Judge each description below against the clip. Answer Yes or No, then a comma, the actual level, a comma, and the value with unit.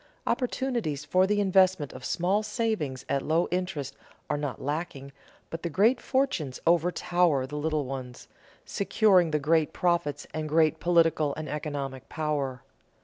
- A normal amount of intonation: Yes, average, 4.0 semitones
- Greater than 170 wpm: No, average, 145 wpm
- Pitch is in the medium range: Yes, medium, 160 Hz